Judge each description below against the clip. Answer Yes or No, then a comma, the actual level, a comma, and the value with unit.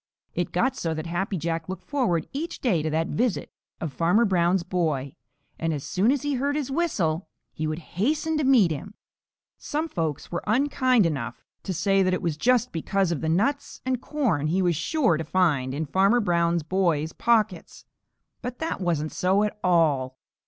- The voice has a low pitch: No, medium, 180 Hz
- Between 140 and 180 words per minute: No, average, 190 wpm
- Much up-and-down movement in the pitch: Yes, wide, 7.0 semitones